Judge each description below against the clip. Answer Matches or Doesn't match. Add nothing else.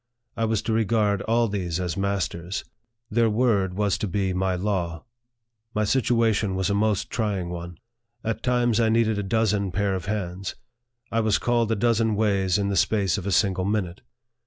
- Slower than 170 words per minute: Doesn't match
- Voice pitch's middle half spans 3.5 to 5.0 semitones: Doesn't match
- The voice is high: Doesn't match